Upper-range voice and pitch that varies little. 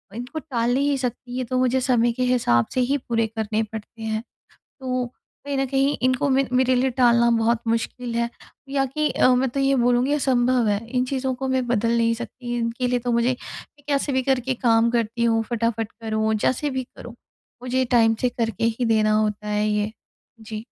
Yes: high, 245 Hz; narrow, 2.3 semitones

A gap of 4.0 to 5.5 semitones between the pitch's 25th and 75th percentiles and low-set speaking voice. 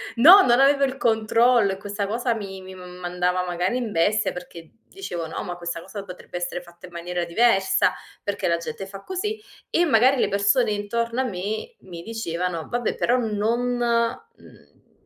No: average, 5.1 semitones; high, 205 Hz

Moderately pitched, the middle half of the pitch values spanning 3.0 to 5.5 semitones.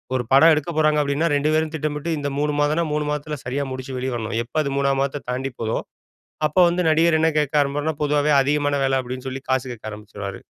No: medium, 145 Hz; narrow, 2.6 semitones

